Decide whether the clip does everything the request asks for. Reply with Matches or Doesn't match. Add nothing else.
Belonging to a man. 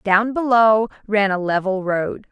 Doesn't match